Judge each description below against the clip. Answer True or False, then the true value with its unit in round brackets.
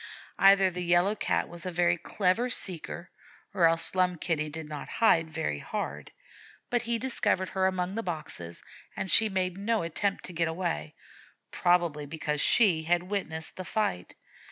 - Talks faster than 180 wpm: False (165 wpm)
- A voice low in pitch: False (180 Hz)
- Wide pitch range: False (3.2 semitones)